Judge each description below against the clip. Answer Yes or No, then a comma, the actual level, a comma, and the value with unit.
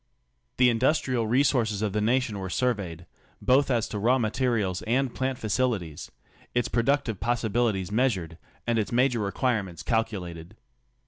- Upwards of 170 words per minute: Yes, average, 180 wpm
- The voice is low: Yes, low, 115 Hz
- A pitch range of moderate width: Yes, average, 4.0 semitones